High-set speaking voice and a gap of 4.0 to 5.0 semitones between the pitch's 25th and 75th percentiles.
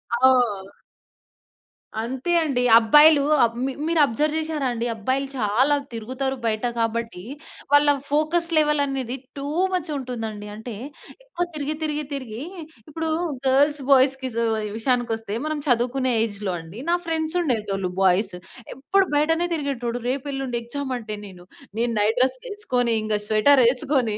Yes: very high, 260 Hz; average, 4.7 semitones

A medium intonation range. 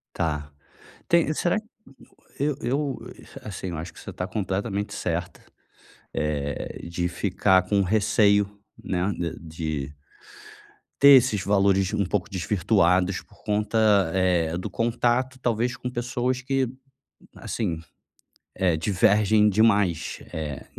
Yes: average, 4.6 semitones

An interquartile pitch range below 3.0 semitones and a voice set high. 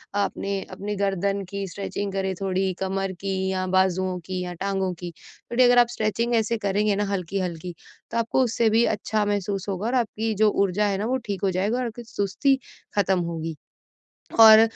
Yes: narrow, 2.5 semitones; high, 200 Hz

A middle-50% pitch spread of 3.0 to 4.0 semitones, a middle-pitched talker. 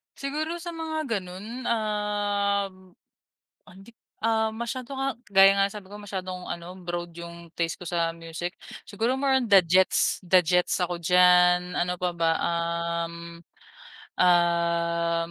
Yes: average, 3.4 semitones; medium, 180 Hz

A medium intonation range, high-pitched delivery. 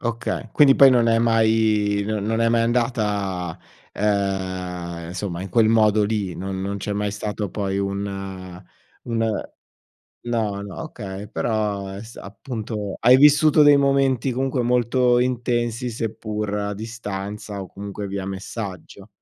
No: average, 3.0 semitones; low, 105 Hz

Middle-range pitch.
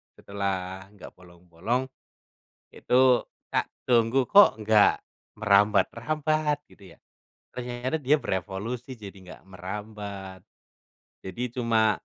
No: low, 105 Hz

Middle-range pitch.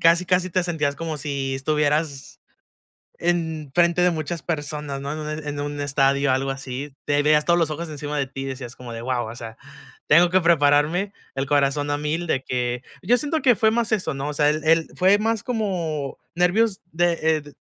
Yes: medium, 150 Hz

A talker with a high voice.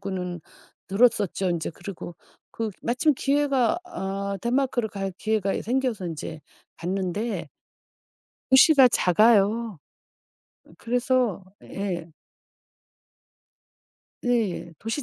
Yes: high, 215 Hz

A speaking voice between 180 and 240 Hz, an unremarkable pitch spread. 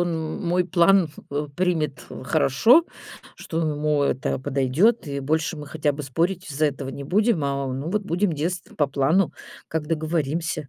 No: medium, 155 Hz; average, 3.7 semitones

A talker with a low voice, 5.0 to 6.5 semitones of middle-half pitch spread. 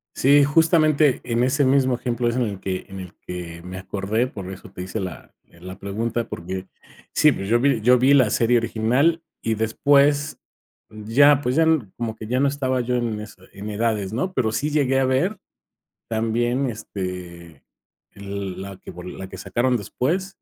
Yes: low, 115 Hz; average, 5.3 semitones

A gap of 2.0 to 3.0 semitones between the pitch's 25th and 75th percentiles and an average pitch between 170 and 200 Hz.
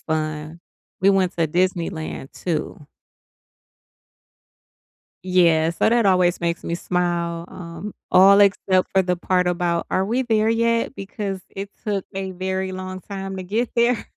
Yes: narrow, 2.6 semitones; medium, 185 Hz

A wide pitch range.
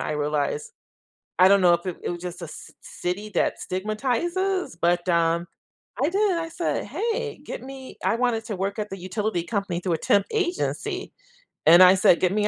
Yes: wide, 7.4 semitones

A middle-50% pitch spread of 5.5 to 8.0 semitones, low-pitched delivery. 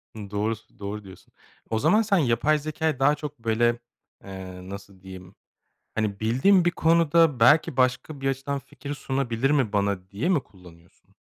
Yes: wide, 6.6 semitones; low, 120 Hz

